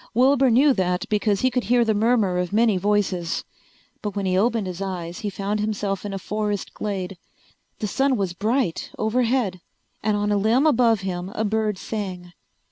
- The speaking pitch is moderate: No, high, 210 Hz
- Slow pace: No, average, 185 wpm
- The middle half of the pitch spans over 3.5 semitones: No, average, 3.2 semitones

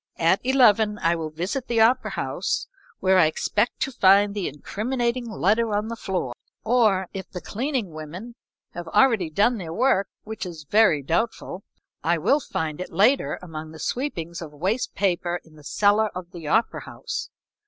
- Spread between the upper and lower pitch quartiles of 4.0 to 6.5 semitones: Yes, wide, 5.5 semitones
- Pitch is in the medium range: No, high, 195 Hz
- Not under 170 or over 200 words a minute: Yes, average, 175 wpm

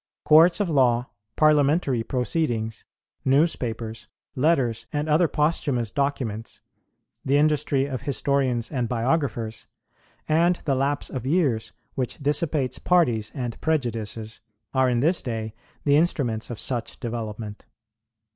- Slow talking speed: Yes, slow, 120 wpm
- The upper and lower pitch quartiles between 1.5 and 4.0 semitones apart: No, average, 4.4 semitones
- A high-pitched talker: No, low, 130 Hz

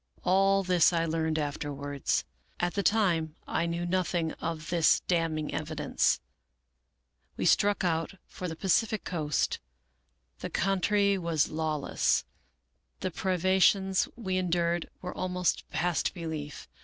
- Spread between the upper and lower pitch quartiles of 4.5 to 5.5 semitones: No, average, 2.9 semitones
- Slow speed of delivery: Yes, slow, 130 wpm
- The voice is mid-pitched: Yes, medium, 170 Hz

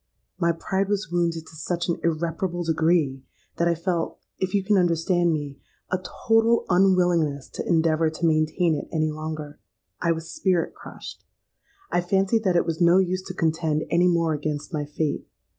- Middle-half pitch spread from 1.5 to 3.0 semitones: Yes, narrow, 2.4 semitones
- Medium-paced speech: Yes, average, 175 wpm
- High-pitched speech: No, medium, 170 Hz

